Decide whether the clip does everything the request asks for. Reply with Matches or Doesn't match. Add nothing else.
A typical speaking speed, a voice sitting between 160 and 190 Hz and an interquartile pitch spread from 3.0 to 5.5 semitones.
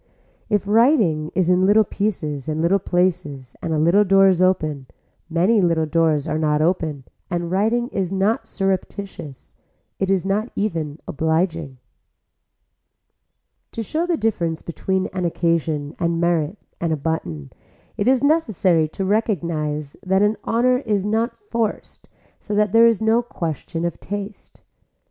Matches